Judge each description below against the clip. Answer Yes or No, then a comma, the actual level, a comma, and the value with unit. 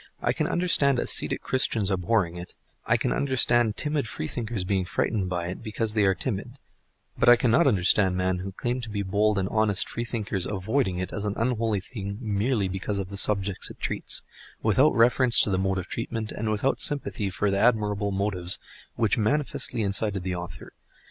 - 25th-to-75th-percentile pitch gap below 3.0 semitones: No, average, 3.5 semitones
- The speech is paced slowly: No, average, 185 wpm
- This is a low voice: Yes, low, 105 Hz